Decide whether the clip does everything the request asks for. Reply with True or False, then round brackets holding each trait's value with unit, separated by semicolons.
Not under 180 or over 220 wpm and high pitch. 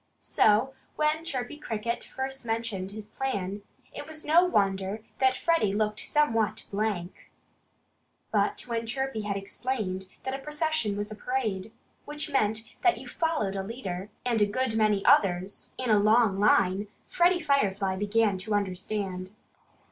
False (145 wpm; 215 Hz)